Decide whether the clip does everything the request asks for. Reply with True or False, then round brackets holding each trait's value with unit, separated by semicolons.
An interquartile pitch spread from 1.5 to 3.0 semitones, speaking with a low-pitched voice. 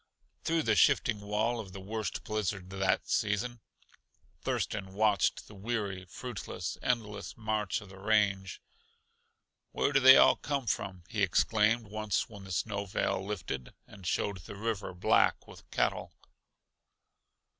True (2.5 semitones; 105 Hz)